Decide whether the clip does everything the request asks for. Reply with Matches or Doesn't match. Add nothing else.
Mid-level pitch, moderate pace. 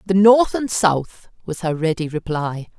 Matches